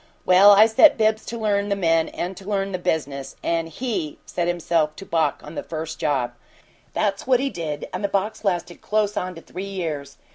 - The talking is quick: Yes, fast, 210 wpm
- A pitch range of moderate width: Yes, average, 4.1 semitones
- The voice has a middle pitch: Yes, medium, 180 Hz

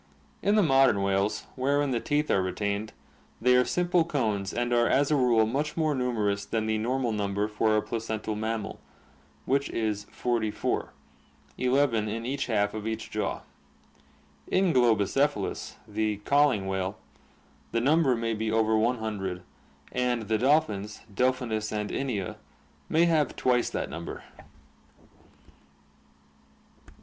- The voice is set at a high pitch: No, low, 115 Hz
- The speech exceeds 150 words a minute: No, average, 140 wpm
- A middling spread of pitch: Yes, average, 3.9 semitones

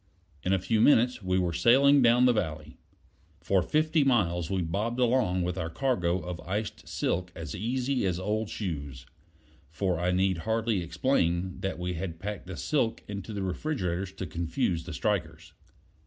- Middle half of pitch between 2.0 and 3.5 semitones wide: No, average, 5.0 semitones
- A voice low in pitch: Yes, very low, 95 Hz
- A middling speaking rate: Yes, average, 170 wpm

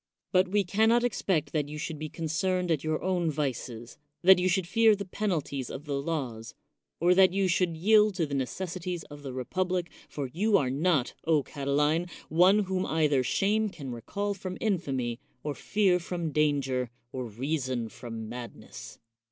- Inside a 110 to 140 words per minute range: No, average, 175 wpm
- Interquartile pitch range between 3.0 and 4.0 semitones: No, average, 5.1 semitones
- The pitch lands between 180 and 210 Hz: No, medium, 160 Hz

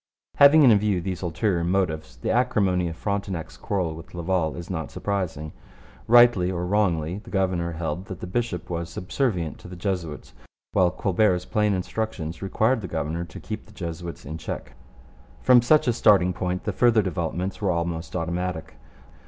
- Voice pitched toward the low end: Yes, very low, 90 Hz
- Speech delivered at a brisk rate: No, average, 170 wpm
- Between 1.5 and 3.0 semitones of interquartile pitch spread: No, average, 3.6 semitones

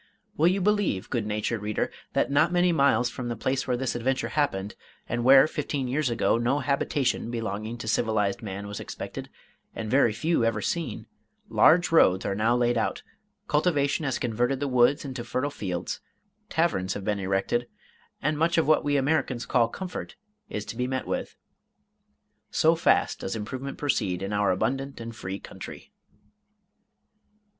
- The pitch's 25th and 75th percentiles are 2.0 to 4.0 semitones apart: No, average, 4.9 semitones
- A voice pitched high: No, low, 120 Hz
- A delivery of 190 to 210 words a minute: No, average, 165 wpm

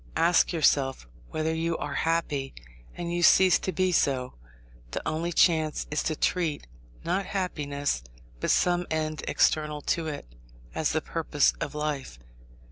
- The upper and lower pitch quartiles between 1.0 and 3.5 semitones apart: Yes, average, 2.9 semitones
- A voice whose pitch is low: No, medium, 155 Hz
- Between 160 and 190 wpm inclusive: No, average, 145 wpm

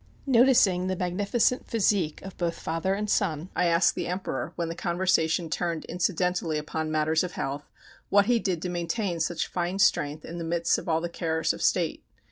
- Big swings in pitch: No, narrow, 2.6 semitones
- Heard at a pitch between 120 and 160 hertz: No, medium, 175 Hz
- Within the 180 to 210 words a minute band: Yes, average, 190 wpm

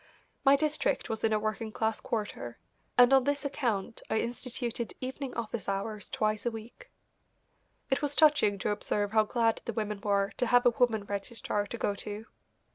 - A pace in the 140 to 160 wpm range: No, average, 180 wpm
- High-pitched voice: Yes, high, 225 Hz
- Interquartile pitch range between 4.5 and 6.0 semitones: No, average, 3.1 semitones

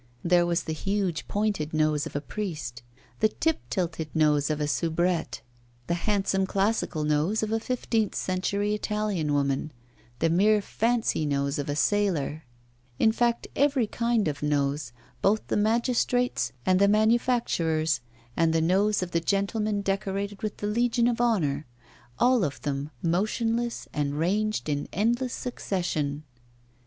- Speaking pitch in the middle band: No, high, 195 Hz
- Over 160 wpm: No, average, 145 wpm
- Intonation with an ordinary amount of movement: No, wide, 5.9 semitones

